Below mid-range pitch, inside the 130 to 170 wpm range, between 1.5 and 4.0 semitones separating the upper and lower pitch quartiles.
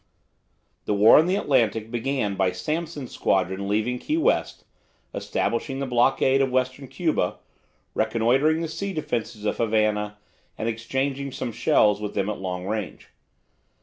No: low, 120 Hz; average, 145 wpm; average, 4.6 semitones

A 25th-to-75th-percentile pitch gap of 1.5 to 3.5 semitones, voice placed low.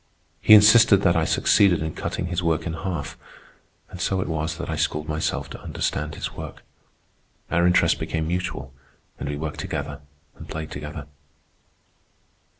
Yes: average, 2.8 semitones; very low, 80 Hz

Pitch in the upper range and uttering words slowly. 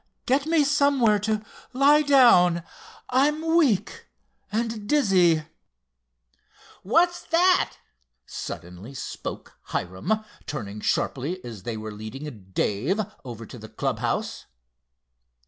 Yes: high, 205 Hz; slow, 105 wpm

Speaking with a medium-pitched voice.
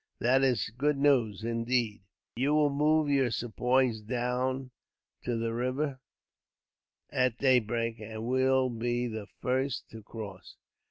No: low, 125 Hz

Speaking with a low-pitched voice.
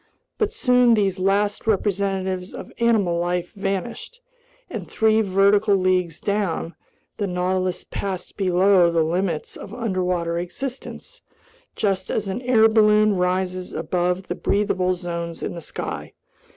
No: high, 190 Hz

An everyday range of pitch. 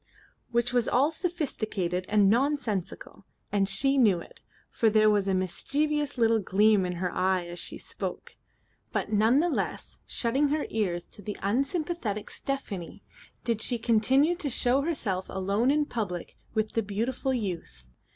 No: wide, 5.7 semitones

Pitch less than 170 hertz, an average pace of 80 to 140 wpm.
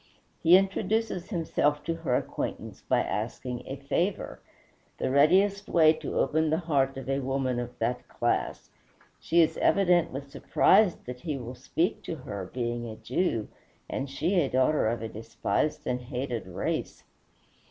No: medium, 140 Hz; average, 155 wpm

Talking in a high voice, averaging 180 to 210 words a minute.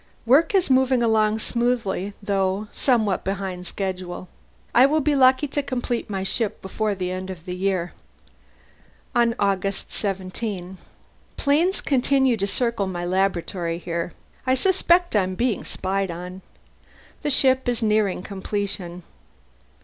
No: high, 200 Hz; slow, 135 wpm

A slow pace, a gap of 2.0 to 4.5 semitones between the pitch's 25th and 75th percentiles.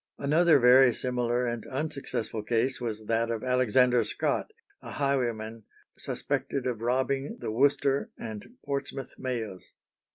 Yes: slow, 125 wpm; average, 3.1 semitones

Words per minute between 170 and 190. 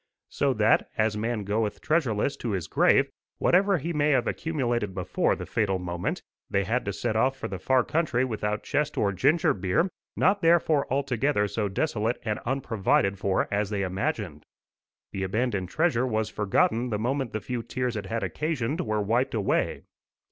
Yes: average, 175 wpm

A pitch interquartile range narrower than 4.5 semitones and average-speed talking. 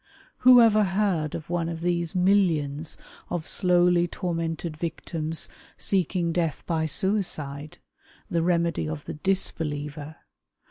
No: narrow, 2.5 semitones; slow, 125 wpm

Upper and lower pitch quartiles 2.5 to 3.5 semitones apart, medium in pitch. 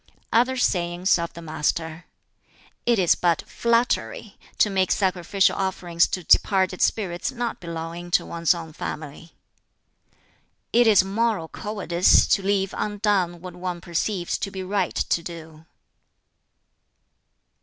Yes: average, 3.1 semitones; medium, 180 Hz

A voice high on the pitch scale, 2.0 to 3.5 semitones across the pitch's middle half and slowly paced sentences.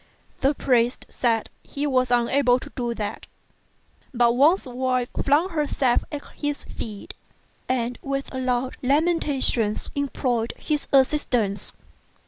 Yes: very high, 255 Hz; average, 2.9 semitones; slow, 115 wpm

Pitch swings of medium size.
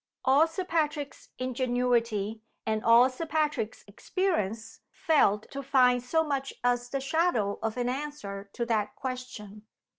Yes: average, 4.7 semitones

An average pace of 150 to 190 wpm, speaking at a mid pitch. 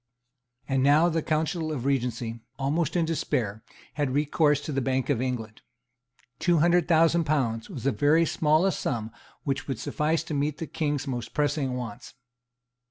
Yes: average, 165 wpm; medium, 145 Hz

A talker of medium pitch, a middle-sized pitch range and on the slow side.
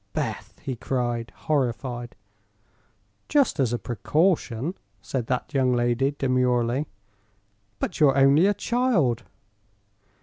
No: low, 130 Hz; average, 3.8 semitones; slow, 105 wpm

